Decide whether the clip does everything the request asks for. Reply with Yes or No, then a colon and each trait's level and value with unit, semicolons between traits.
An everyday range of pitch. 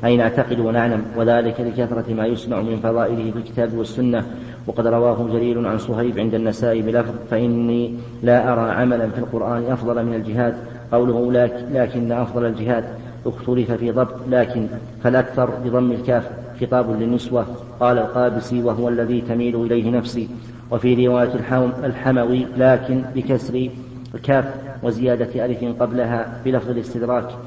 No: narrow, 0.9 semitones